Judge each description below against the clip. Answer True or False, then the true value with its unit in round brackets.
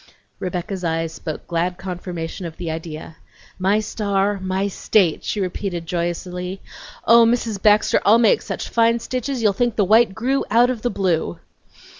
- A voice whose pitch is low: False (195 Hz)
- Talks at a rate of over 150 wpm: True (160 wpm)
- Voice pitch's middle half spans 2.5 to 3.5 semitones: False (4.0 semitones)